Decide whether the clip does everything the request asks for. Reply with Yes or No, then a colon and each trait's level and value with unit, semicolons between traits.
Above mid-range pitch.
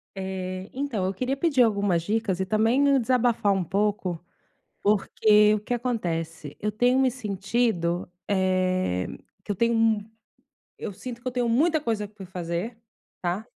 Yes: high, 210 Hz